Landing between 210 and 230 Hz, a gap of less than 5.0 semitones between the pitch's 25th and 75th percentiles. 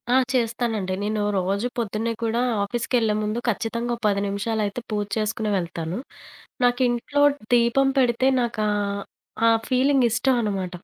Yes: high, 225 Hz; average, 2.7 semitones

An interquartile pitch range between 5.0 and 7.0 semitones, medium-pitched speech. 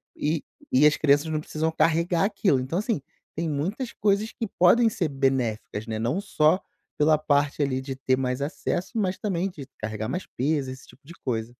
Yes: average, 5.3 semitones; medium, 150 Hz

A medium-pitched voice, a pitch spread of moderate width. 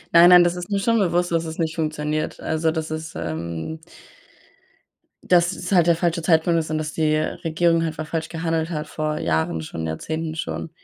No: medium, 160 Hz; narrow, 1.8 semitones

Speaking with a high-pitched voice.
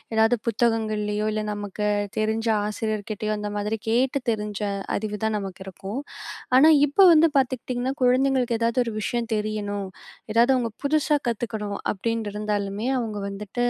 Yes: high, 220 Hz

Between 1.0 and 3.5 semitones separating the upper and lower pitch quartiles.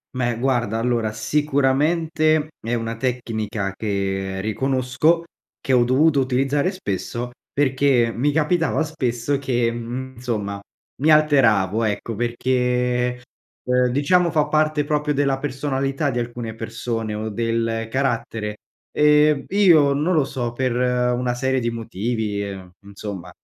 No: average, 3.9 semitones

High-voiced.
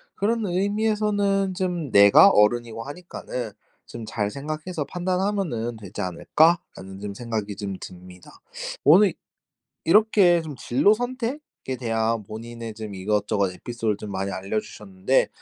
No: low, 120 Hz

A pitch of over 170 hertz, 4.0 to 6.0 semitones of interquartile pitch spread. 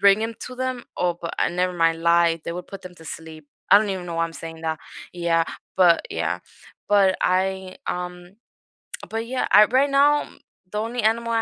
Yes: medium, 185 Hz; average, 4.7 semitones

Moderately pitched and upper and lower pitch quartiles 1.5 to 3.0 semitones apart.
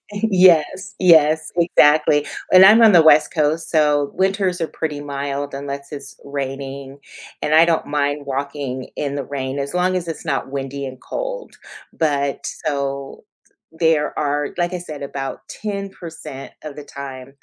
No: medium, 150 Hz; average, 3.4 semitones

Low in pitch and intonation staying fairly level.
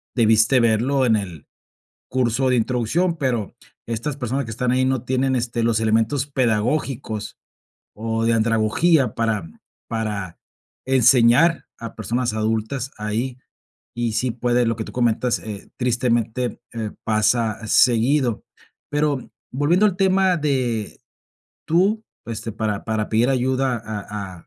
No: low, 120 Hz; average, 3.1 semitones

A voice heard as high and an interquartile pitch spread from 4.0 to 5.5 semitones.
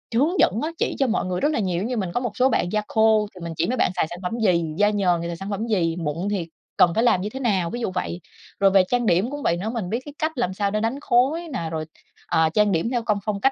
Yes: high, 205 Hz; average, 5.1 semitones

